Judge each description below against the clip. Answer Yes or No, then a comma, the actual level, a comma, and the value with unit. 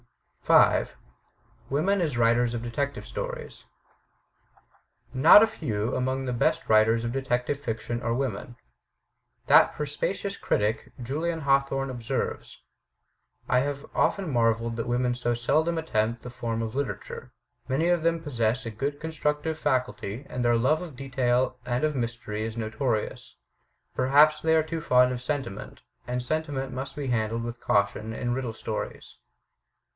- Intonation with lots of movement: No, average, 3.8 semitones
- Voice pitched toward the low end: Yes, low, 125 Hz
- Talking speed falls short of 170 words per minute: Yes, average, 150 wpm